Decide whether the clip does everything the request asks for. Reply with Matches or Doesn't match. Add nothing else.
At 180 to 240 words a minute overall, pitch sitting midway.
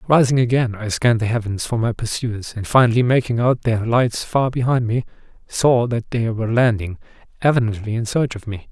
Doesn't match